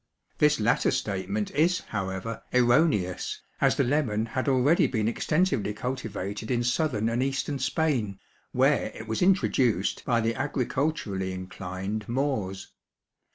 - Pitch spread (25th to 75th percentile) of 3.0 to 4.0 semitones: No, average, 5.0 semitones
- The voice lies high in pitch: No, low, 115 Hz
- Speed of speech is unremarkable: No, slow, 125 wpm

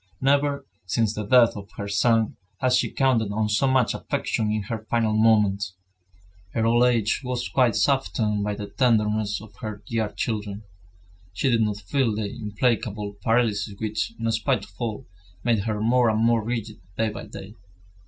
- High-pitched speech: No, low, 110 Hz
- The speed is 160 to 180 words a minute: Yes, average, 175 wpm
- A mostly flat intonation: Yes, narrow, 2.3 semitones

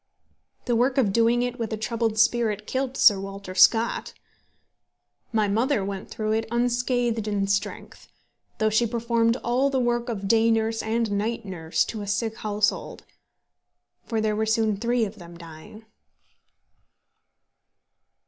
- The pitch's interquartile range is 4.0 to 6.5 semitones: No, narrow, 2.4 semitones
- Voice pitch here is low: No, high, 225 Hz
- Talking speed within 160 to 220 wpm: No, average, 150 wpm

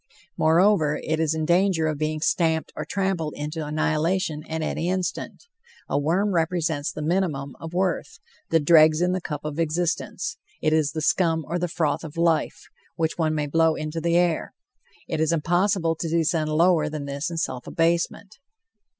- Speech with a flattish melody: Yes, narrow, 2.0 semitones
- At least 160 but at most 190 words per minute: Yes, average, 175 wpm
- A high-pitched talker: No, medium, 160 Hz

